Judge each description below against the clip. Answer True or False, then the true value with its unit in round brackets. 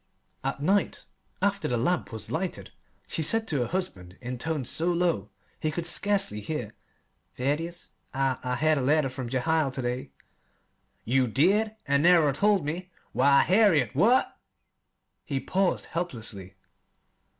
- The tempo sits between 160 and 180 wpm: False (150 wpm)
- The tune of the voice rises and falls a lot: True (5.9 semitones)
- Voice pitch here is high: False (150 Hz)